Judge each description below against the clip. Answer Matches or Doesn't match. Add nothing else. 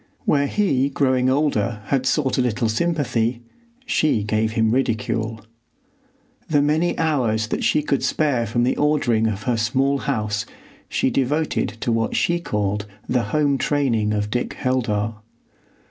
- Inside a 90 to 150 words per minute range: Matches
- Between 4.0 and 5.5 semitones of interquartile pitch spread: Matches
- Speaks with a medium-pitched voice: Doesn't match